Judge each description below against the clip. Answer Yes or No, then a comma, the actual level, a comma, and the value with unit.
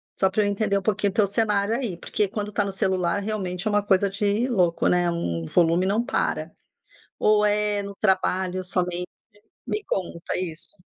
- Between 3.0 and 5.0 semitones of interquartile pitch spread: No, narrow, 2.5 semitones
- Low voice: No, high, 200 Hz